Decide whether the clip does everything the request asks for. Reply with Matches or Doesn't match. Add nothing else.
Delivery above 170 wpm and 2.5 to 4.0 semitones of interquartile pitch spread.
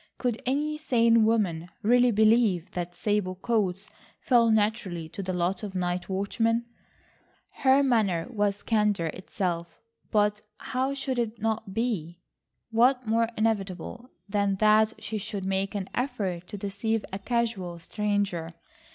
Doesn't match